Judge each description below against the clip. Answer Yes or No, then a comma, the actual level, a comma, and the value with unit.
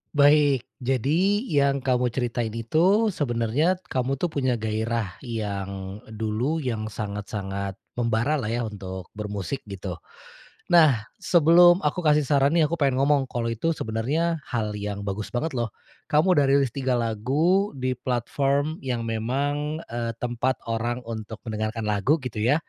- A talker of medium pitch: No, low, 125 Hz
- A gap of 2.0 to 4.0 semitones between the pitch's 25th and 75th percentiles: No, average, 4.9 semitones